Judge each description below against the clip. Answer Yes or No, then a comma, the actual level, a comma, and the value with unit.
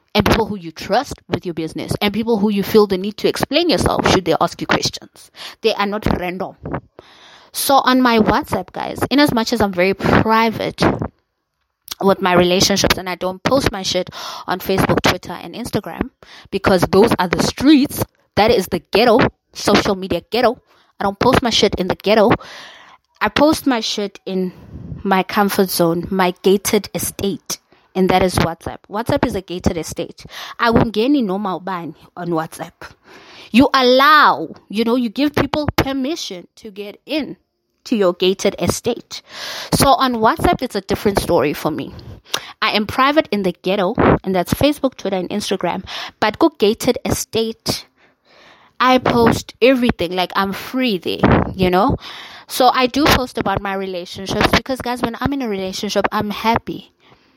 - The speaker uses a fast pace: No, average, 175 wpm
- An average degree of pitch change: Yes, average, 4.6 semitones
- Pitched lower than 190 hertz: No, high, 205 Hz